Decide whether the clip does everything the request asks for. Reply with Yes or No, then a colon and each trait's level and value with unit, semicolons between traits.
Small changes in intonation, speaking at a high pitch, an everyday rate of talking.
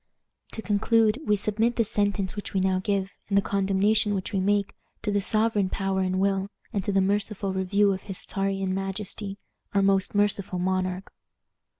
Yes: narrow, 1.4 semitones; high, 200 Hz; average, 180 wpm